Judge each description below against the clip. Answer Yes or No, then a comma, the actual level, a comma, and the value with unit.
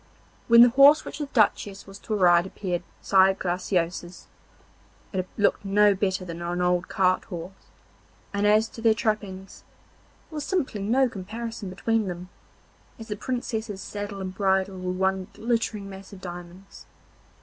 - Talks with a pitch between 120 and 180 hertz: No, high, 195 Hz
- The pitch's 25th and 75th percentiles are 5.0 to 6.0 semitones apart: No, average, 2.9 semitones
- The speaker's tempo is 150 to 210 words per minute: Yes, average, 155 wpm